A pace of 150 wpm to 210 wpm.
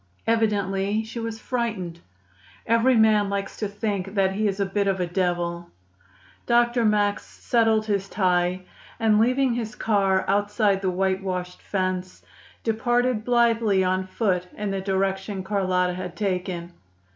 No: average, 140 wpm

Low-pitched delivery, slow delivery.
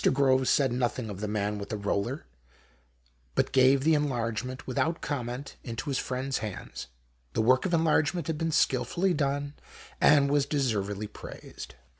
No: low, 130 Hz; average, 160 wpm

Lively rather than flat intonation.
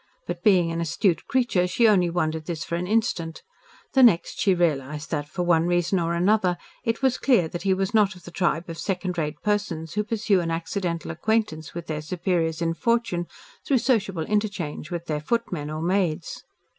No: average, 4.0 semitones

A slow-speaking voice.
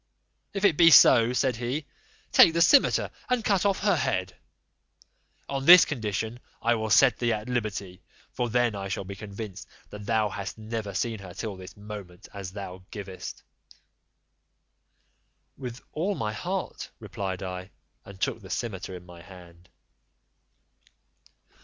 No: average, 150 wpm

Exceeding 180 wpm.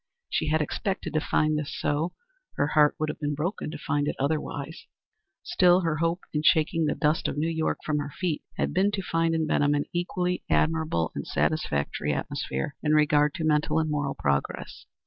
Yes: average, 195 wpm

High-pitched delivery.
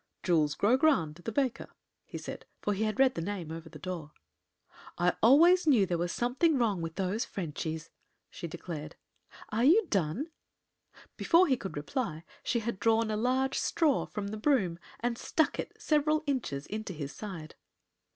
Yes: high, 210 Hz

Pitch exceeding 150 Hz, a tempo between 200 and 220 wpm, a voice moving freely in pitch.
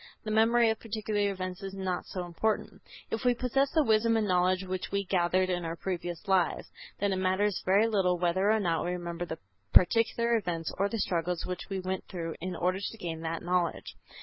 No: medium, 185 Hz; fast, 205 wpm; average, 3.3 semitones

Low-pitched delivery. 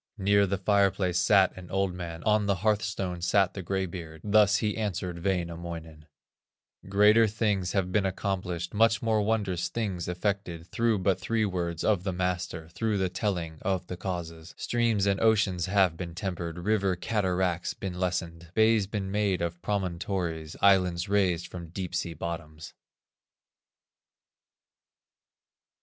Yes: very low, 95 Hz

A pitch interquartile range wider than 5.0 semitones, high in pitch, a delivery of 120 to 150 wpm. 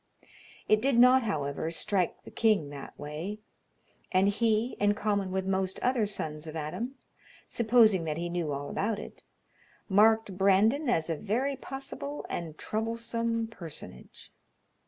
Yes: wide, 5.4 semitones; high, 205 Hz; average, 140 wpm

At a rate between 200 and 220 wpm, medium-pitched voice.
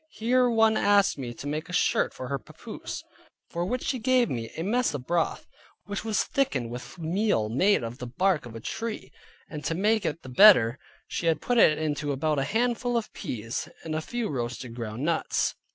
Yes: fast, 205 wpm; medium, 165 Hz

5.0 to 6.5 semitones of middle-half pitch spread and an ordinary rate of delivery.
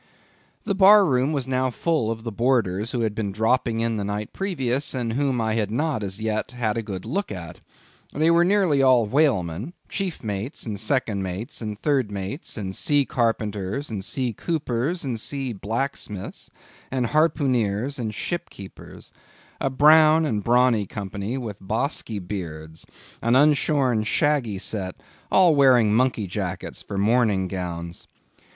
Yes: average, 5.3 semitones; average, 160 wpm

